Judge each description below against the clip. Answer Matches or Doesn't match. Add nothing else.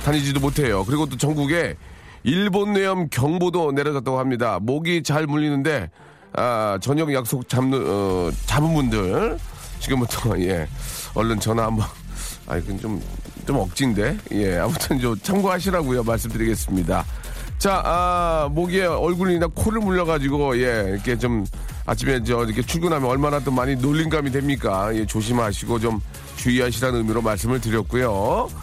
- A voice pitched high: Doesn't match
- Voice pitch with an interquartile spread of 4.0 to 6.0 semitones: Matches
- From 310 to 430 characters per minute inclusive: Matches